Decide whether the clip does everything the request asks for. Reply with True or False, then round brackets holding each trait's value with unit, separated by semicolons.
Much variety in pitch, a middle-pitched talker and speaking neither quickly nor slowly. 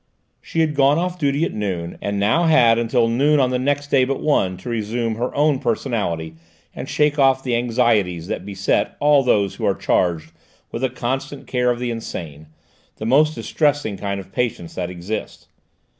False (5.7 semitones; 120 Hz; 190 wpm)